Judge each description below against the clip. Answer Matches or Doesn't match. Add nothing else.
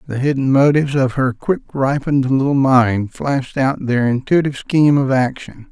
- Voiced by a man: Matches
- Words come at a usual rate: Matches